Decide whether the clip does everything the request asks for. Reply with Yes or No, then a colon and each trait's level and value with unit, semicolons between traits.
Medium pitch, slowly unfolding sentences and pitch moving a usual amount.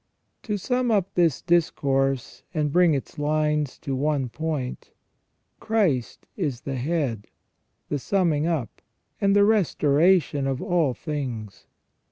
Yes: medium, 150 Hz; slow, 125 wpm; average, 4.5 semitones